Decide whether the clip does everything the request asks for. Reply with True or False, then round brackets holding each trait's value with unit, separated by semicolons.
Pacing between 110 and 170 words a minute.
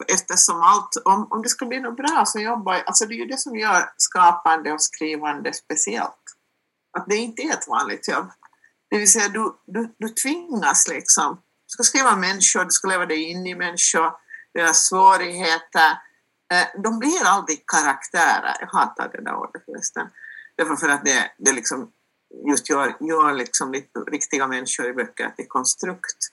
False (180 wpm)